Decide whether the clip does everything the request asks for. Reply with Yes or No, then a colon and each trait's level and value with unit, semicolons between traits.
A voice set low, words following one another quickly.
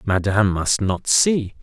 No: low, 110 Hz; average, 150 wpm